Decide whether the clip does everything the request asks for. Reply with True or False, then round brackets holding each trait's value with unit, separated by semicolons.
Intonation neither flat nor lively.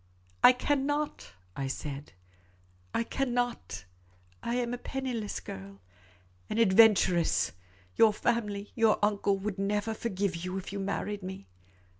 False (6.3 semitones)